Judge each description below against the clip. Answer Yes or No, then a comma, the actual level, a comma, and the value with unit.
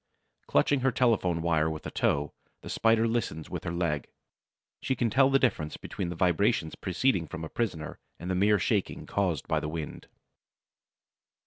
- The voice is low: Yes, very low, 90 Hz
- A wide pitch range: Yes, wide, 6.3 semitones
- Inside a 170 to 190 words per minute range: Yes, average, 175 wpm